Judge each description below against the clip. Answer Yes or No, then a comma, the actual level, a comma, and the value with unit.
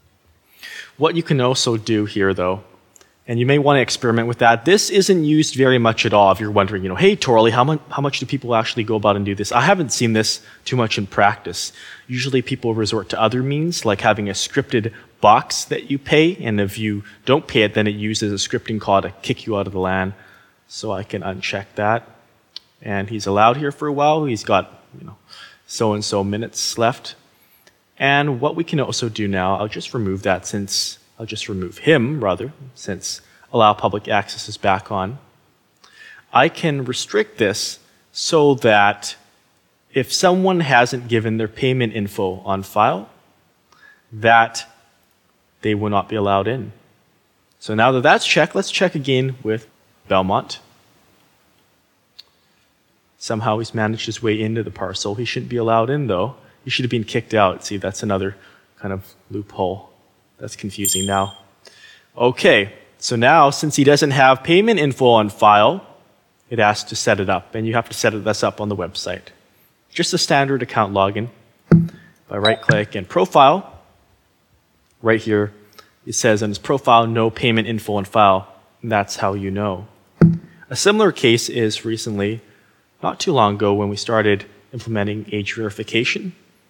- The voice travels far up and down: No, average, 3.8 semitones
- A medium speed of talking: Yes, average, 180 wpm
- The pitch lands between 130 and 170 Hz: No, low, 110 Hz